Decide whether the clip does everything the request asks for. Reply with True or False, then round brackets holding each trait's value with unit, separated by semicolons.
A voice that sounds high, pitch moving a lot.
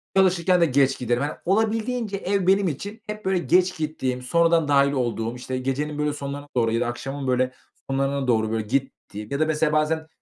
False (145 Hz; 5.7 semitones)